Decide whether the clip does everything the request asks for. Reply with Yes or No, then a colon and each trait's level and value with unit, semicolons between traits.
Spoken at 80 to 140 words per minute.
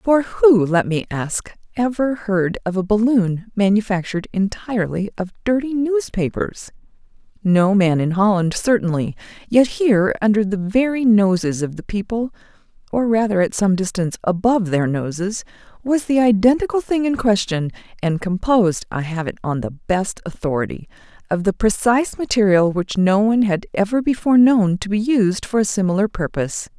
No: average, 155 wpm